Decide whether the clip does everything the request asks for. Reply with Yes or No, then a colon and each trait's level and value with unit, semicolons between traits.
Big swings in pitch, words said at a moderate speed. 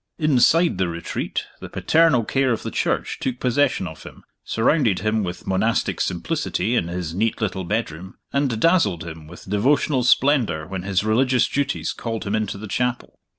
Yes: wide, 5.7 semitones; average, 170 wpm